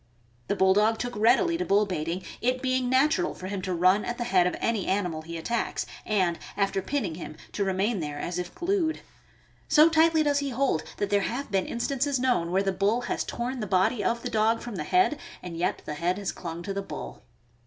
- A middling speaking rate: No, fast, 220 wpm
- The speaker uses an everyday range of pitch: No, wide, 5.7 semitones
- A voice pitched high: Yes, high, 210 Hz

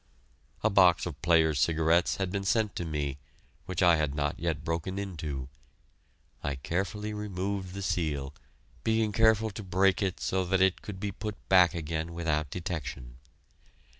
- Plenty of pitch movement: No, average, 3.8 semitones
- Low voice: Yes, very low, 90 Hz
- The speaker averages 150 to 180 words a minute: Yes, average, 160 wpm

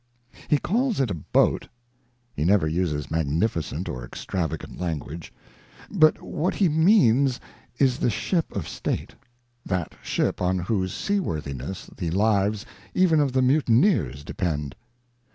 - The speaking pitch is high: No, low, 100 Hz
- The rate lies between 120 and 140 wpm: Yes, slow, 135 wpm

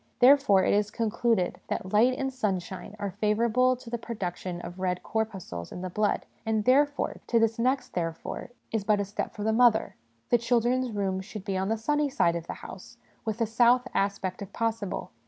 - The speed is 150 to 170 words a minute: No, fast, 205 wpm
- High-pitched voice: Yes, high, 220 Hz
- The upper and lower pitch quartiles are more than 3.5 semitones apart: Yes, average, 3.9 semitones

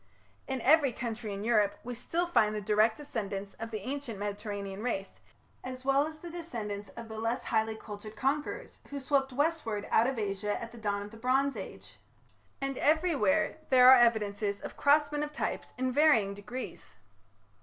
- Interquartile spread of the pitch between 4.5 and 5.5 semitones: Yes, average, 4.9 semitones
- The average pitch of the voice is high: Yes, high, 235 Hz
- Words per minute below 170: No, average, 175 wpm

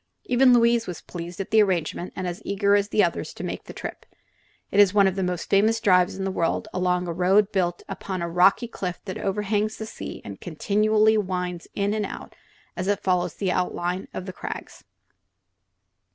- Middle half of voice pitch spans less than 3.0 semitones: Yes, narrow, 2.5 semitones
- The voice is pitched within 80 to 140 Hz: No, high, 190 Hz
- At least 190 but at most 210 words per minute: Yes, average, 200 wpm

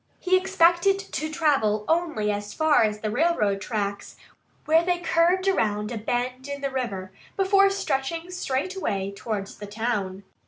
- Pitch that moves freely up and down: Yes, wide, 8.5 semitones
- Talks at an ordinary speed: Yes, average, 155 wpm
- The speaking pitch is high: Yes, very high, 265 Hz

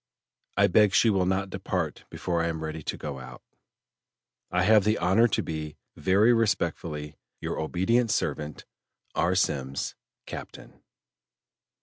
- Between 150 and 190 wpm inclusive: No, slow, 135 wpm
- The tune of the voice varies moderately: Yes, average, 4.7 semitones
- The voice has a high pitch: No, very low, 90 Hz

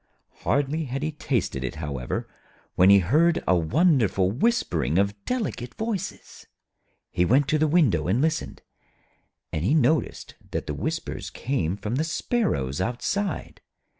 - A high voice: No, low, 125 Hz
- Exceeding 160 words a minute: No, average, 140 wpm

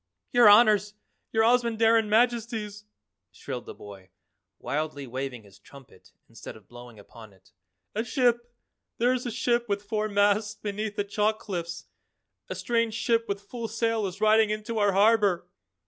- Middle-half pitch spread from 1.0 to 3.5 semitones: No, average, 3.9 semitones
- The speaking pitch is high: Yes, high, 210 Hz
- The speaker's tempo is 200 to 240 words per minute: No, average, 155 wpm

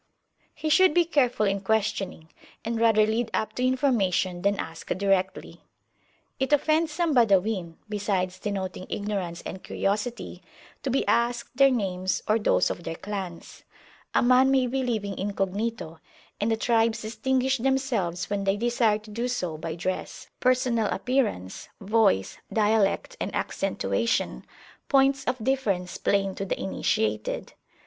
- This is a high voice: Yes, high, 215 Hz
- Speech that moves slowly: No, average, 145 wpm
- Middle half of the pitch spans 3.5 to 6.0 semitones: Yes, average, 4.8 semitones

